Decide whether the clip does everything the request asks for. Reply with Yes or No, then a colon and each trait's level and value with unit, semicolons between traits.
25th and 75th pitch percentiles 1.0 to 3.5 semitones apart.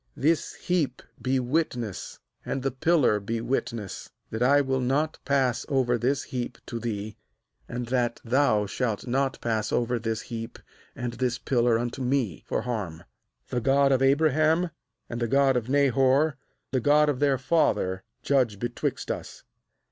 Yes: average, 3.0 semitones